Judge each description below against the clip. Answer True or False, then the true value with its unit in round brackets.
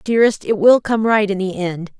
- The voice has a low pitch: False (205 Hz)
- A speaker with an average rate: False (240 wpm)